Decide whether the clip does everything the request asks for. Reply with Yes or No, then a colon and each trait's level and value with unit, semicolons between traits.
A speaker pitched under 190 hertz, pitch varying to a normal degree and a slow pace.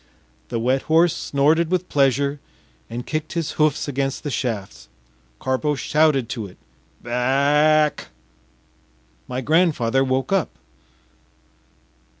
Yes: medium, 140 Hz; average, 3.6 semitones; slow, 115 wpm